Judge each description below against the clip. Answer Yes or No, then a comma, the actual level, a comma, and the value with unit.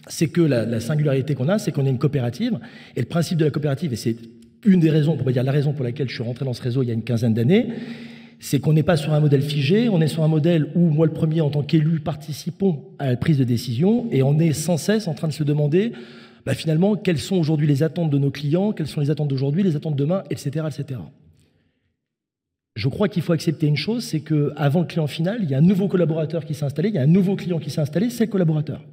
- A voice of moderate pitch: Yes, medium, 155 Hz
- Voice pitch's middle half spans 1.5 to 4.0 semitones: Yes, average, 3.6 semitones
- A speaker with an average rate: No, fast, 270 wpm